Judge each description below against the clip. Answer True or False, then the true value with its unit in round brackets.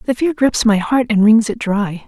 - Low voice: False (225 Hz)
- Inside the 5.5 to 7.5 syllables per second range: False (4.8 syllables/s)